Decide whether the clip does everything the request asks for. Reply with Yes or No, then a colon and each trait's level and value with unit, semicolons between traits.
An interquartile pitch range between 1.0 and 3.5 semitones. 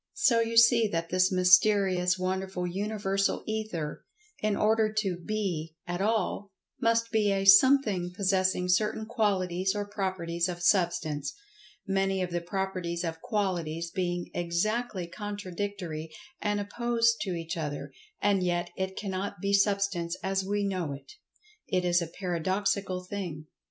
Yes: average, 2.9 semitones